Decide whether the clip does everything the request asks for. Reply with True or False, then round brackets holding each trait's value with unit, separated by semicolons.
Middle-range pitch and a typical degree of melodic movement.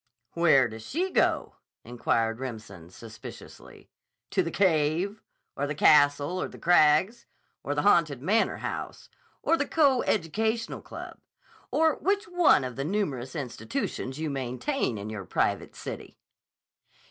False (150 Hz; 9.0 semitones)